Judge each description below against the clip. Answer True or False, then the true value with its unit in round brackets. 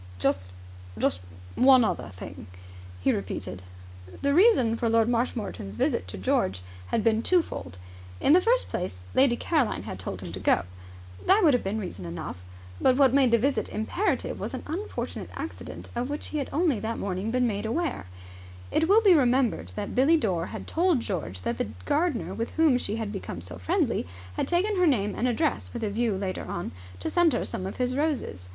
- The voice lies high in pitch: True (230 Hz)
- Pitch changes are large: True (8.3 semitones)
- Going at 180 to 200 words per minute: True (195 wpm)